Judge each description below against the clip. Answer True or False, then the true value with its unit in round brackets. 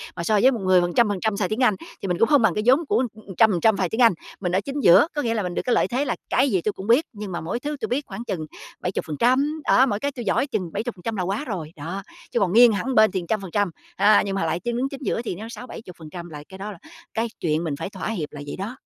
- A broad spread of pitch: False (4.9 semitones)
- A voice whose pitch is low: False (210 Hz)